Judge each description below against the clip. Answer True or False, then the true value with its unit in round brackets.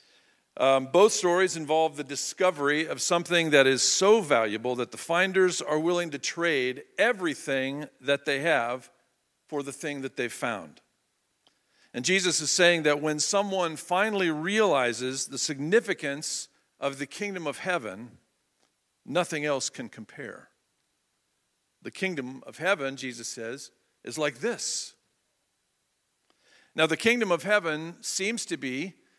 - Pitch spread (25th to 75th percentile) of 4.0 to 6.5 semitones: True (4.8 semitones)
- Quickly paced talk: False (135 wpm)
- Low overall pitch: False (155 Hz)